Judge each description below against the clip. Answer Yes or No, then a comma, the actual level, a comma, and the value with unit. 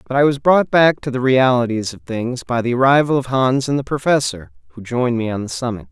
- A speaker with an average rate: No, fast, 245 wpm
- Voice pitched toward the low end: Yes, low, 125 Hz